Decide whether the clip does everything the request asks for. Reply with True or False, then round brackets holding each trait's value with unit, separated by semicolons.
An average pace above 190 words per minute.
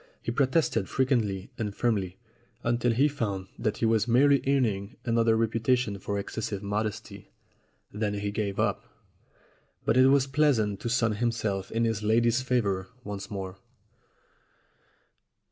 False (140 wpm)